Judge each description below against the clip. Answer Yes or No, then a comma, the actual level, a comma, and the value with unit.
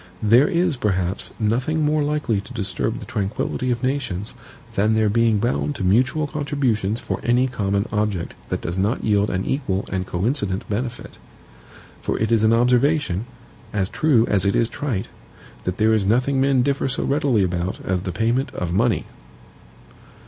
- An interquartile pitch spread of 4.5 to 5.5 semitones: Yes, average, 4.9 semitones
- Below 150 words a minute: No, average, 170 wpm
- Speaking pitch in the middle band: No, low, 115 Hz